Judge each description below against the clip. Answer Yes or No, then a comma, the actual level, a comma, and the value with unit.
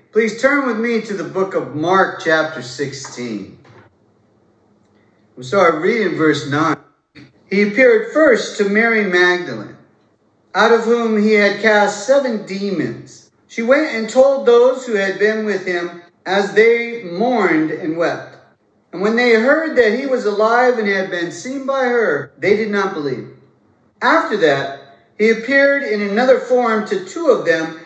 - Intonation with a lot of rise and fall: Yes, wide, 6.9 semitones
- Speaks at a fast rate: No, average, 160 wpm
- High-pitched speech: Yes, high, 205 Hz